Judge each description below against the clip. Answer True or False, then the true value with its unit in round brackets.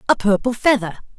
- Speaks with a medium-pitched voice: False (220 Hz)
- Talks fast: False (150 wpm)